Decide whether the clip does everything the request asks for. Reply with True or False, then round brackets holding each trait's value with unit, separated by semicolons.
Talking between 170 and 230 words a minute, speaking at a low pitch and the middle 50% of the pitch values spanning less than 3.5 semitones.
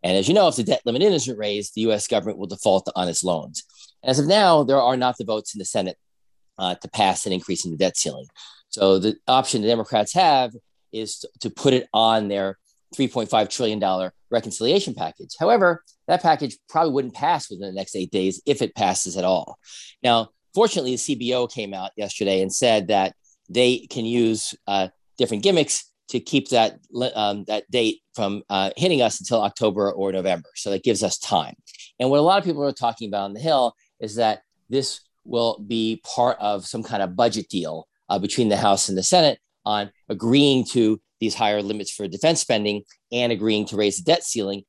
False (205 wpm; 110 Hz; 4.1 semitones)